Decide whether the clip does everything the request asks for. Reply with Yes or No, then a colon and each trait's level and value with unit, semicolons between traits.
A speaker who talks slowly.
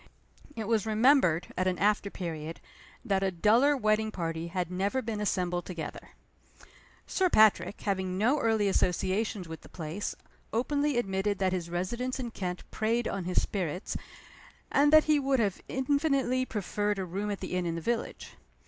No: average, 165 wpm